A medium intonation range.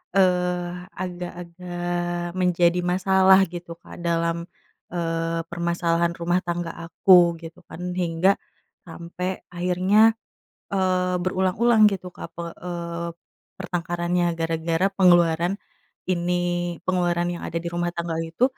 No: narrow, 1.2 semitones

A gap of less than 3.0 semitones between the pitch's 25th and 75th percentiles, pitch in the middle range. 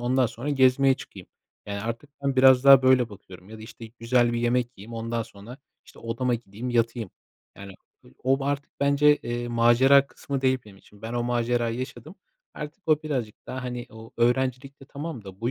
No: narrow, 2.6 semitones; low, 120 Hz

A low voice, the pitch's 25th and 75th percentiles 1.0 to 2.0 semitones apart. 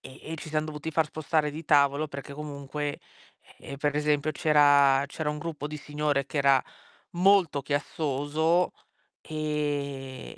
No: medium, 150 Hz; narrow, 1.6 semitones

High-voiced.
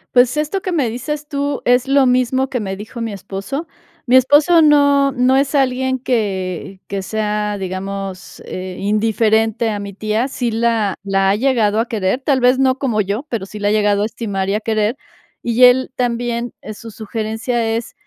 Yes: high, 230 Hz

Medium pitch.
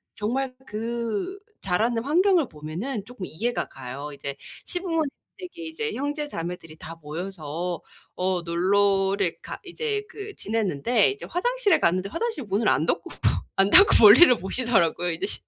No: high, 220 Hz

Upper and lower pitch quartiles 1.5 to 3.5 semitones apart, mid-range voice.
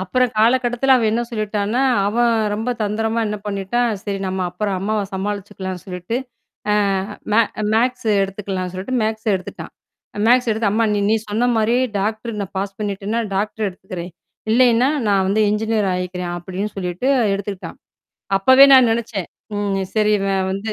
No: average, 2.8 semitones; high, 210 Hz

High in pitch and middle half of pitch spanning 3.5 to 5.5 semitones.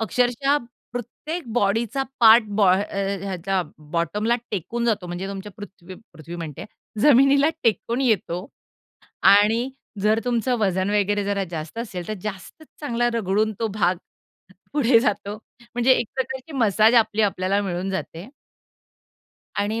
Yes: high, 210 Hz; average, 3.8 semitones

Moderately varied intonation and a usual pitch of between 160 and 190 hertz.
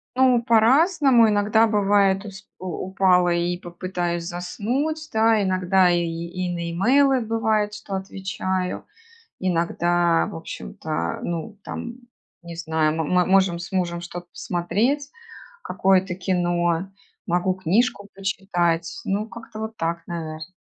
Yes: average, 3.8 semitones; medium, 185 Hz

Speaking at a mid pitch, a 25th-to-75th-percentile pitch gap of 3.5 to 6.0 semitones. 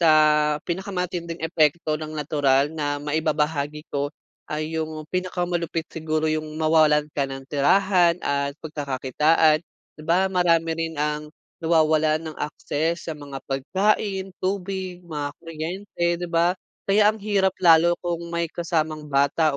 No: medium, 160 Hz; narrow, 2.4 semitones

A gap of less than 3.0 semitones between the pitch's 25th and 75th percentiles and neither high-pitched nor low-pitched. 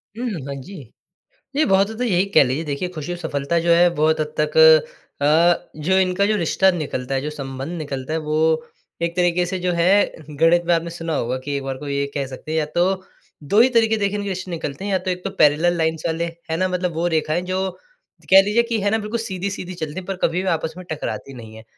No: average, 3.7 semitones; medium, 170 Hz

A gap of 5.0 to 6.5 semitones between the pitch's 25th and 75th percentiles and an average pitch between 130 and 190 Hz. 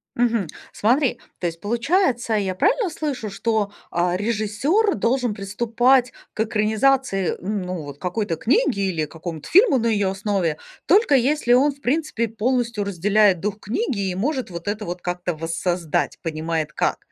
No: wide, 5.5 semitones; high, 210 Hz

